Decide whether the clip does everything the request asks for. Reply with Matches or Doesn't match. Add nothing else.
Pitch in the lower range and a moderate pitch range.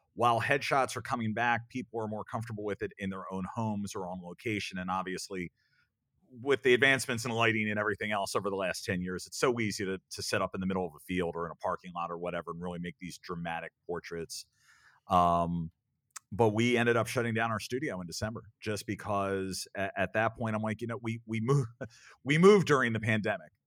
Matches